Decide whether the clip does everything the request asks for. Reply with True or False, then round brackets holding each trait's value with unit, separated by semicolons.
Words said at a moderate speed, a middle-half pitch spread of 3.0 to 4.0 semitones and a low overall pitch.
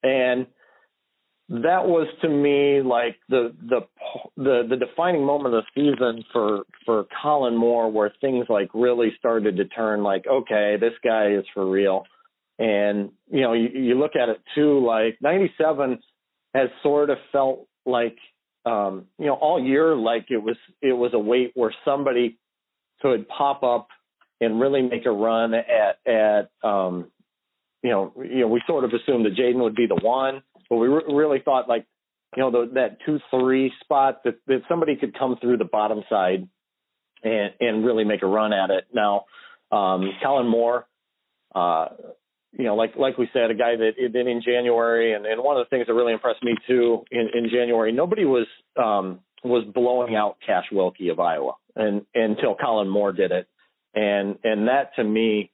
True (185 wpm; 3.4 semitones; 120 Hz)